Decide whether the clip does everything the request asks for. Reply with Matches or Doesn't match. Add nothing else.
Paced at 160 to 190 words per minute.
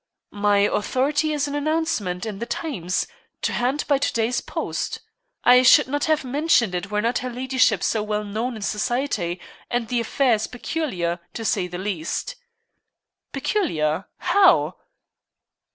Doesn't match